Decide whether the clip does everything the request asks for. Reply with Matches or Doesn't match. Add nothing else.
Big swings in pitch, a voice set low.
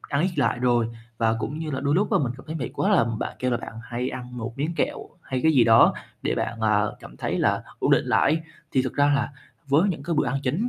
Doesn't match